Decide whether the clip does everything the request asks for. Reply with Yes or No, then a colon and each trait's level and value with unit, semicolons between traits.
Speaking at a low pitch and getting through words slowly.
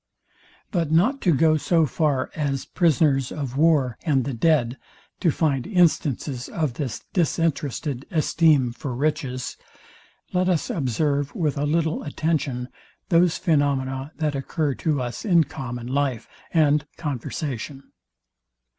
No: medium, 145 Hz; slow, 130 wpm